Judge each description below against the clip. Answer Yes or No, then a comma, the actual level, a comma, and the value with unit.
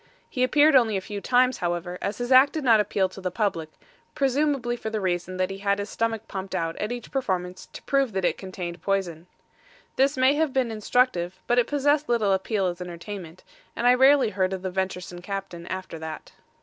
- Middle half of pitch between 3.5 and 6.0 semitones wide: Yes, wide, 5.4 semitones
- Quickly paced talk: Yes, fast, 215 wpm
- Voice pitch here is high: Yes, high, 200 Hz